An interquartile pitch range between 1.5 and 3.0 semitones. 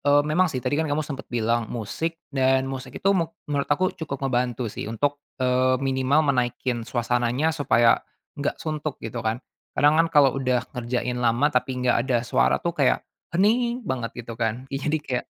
No: average, 3.5 semitones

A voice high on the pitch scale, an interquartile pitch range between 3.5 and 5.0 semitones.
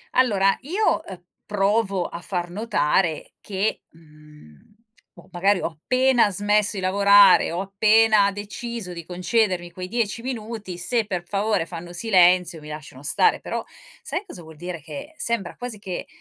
Yes: high, 195 Hz; average, 3.9 semitones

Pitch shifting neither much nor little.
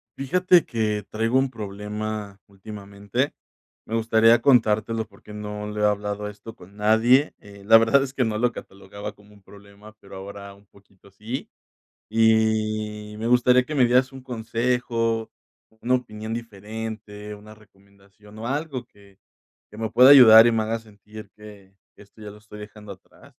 No: narrow, 1.9 semitones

